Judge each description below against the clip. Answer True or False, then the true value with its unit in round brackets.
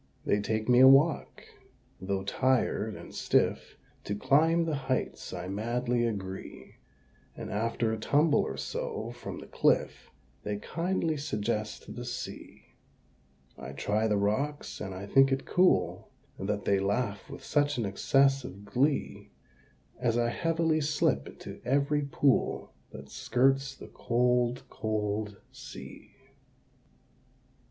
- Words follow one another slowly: True (130 wpm)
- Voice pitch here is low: True (120 Hz)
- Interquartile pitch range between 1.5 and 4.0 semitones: False (5.2 semitones)